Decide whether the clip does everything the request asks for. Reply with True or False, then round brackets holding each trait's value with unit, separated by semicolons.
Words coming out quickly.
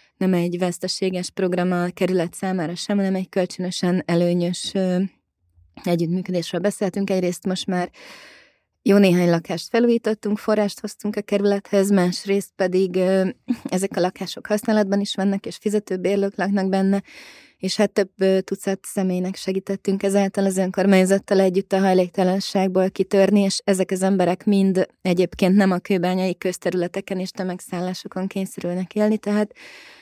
False (130 wpm)